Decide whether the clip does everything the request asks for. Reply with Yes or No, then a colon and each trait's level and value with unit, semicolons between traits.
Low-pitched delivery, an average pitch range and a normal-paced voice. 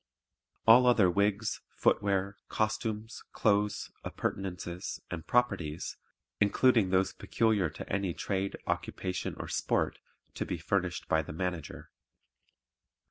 No: low, 100 Hz; average, 3.1 semitones; slow, 110 wpm